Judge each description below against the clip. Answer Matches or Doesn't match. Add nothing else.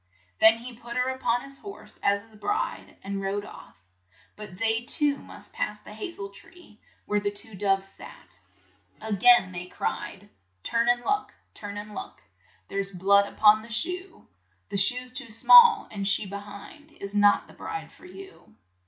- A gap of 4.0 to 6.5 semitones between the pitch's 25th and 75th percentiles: Matches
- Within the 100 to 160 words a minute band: Doesn't match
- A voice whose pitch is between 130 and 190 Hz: Doesn't match